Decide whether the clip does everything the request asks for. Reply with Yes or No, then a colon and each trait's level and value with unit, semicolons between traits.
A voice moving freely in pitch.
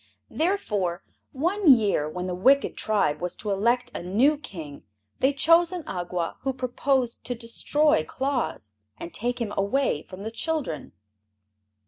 Yes: wide, 7.3 semitones